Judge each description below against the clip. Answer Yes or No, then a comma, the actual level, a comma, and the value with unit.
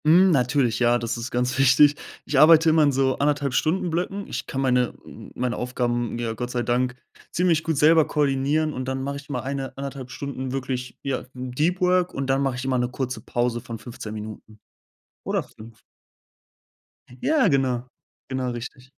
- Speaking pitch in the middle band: No, low, 130 Hz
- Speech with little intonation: No, average, 3.1 semitones